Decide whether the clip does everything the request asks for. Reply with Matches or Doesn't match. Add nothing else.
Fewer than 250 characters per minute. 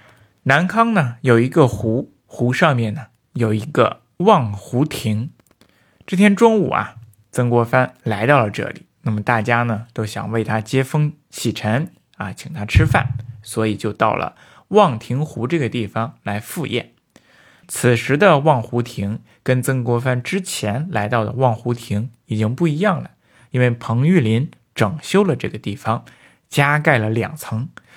Matches